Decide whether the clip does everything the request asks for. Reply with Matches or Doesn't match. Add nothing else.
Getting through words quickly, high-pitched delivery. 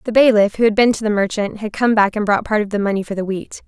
Matches